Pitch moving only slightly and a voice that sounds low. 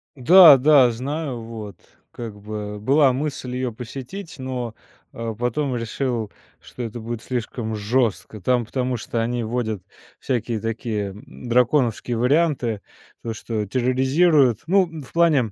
No: average, 3.0 semitones; low, 120 Hz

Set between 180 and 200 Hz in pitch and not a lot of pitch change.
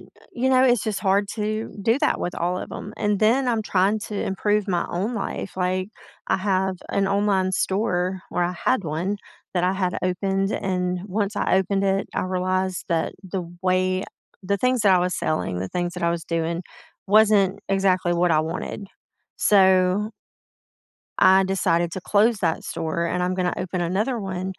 Yes: high, 190 Hz; narrow, 2.2 semitones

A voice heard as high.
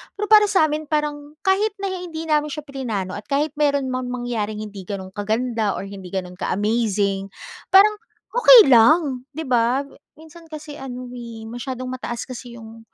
Yes: very high, 255 Hz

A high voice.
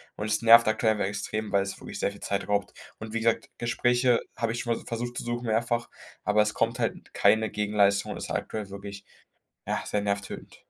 No: low, 110 Hz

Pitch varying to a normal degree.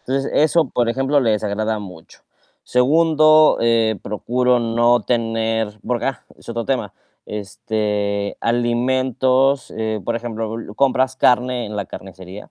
Yes: average, 3.2 semitones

